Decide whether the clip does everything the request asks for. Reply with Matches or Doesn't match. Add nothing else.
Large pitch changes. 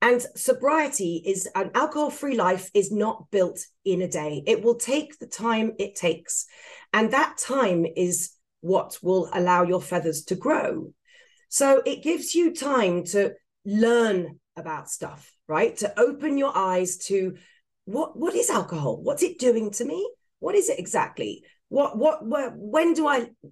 Matches